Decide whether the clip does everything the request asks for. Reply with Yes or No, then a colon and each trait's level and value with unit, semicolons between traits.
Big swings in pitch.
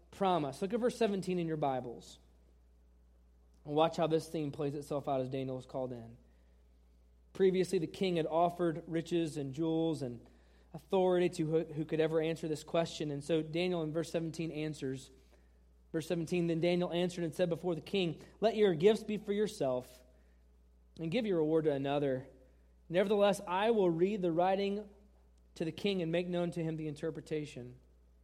Yes: wide, 5.9 semitones